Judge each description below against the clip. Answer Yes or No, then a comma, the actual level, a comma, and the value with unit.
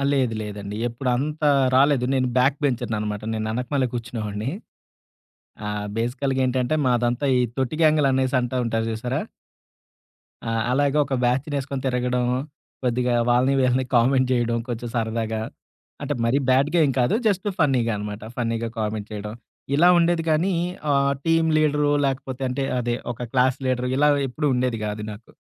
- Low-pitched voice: Yes, low, 125 Hz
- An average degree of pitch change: Yes, average, 3.1 semitones